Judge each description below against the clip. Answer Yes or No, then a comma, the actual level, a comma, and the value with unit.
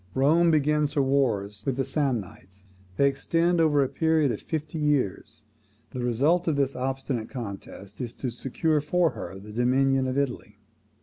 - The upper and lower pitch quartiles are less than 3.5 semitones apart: No, average, 3.8 semitones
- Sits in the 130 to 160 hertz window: Yes, low, 135 Hz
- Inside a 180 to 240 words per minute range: No, average, 165 wpm